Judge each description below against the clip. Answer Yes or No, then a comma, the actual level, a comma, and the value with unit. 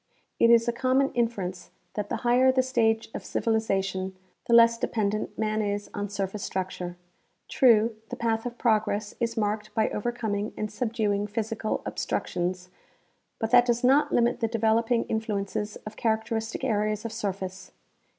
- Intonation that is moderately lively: No, narrow, 2.2 semitones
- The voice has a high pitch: Yes, high, 220 Hz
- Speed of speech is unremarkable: Yes, average, 155 wpm